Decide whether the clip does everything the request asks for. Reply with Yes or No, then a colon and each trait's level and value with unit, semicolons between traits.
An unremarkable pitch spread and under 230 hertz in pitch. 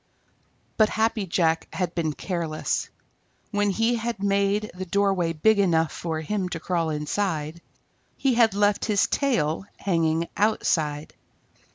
Yes: average, 4.2 semitones; medium, 185 Hz